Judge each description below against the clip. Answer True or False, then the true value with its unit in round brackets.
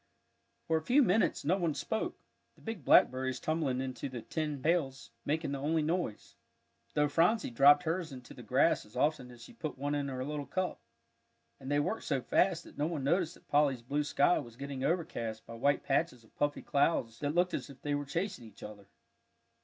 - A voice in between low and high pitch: True (145 Hz)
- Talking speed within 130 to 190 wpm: False (205 wpm)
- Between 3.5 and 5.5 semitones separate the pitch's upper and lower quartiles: True (3.9 semitones)